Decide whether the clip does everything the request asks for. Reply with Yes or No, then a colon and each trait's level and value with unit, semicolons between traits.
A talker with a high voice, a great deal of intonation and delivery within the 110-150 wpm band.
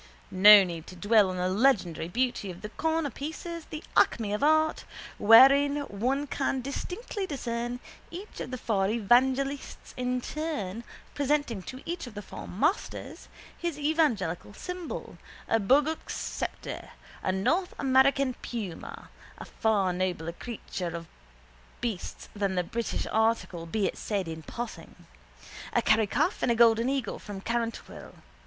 Yes: high, 235 Hz; wide, 6.0 semitones; average, 145 wpm